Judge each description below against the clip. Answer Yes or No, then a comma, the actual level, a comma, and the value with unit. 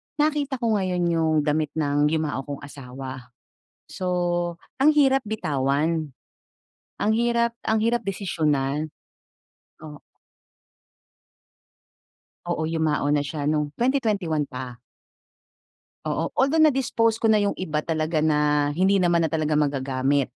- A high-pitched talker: No, medium, 160 Hz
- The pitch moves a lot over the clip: Yes, wide, 6.5 semitones